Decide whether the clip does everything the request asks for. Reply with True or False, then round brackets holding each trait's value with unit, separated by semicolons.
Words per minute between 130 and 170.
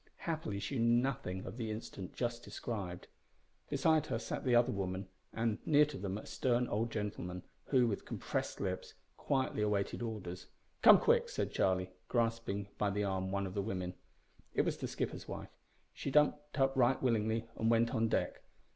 False (180 wpm)